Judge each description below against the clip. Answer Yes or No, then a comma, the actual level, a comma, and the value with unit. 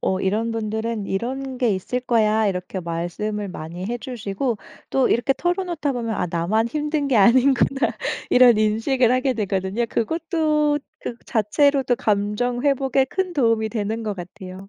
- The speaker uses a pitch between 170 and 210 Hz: No, high, 230 Hz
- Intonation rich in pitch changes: No, average, 4.5 semitones